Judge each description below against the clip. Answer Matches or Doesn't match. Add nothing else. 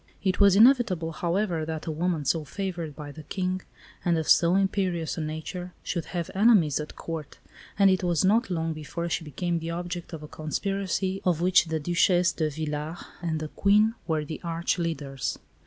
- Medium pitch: Matches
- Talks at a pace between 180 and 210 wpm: Matches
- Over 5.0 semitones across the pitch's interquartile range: Doesn't match